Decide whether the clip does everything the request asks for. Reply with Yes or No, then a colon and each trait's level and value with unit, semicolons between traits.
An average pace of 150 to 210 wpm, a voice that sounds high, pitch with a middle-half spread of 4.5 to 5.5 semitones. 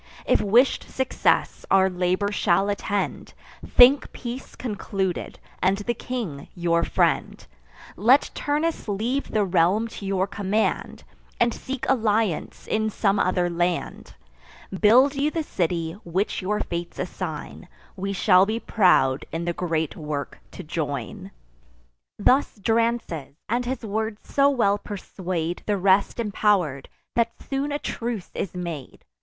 No: slow, 135 wpm; high, 200 Hz; average, 4.8 semitones